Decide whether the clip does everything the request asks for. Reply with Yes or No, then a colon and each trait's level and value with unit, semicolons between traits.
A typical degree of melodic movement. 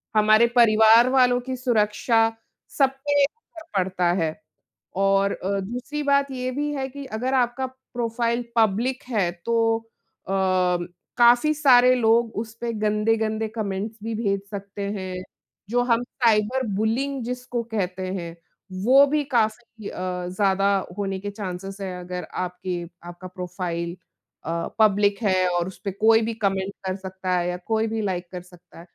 Yes: average, 4.2 semitones